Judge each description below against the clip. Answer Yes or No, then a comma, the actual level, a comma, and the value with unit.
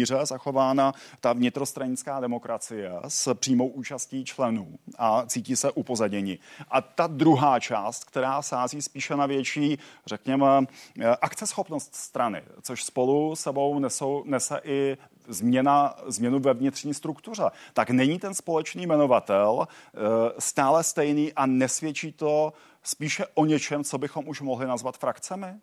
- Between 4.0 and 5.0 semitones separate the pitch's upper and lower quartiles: No, average, 2.8 semitones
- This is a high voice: No, medium, 140 Hz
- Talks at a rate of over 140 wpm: No, average, 125 wpm